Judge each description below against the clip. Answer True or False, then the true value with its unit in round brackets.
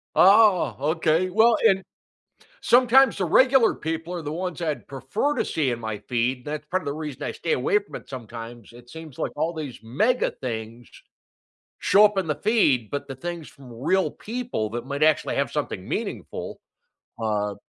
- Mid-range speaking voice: True (155 Hz)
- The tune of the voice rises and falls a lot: True (7.7 semitones)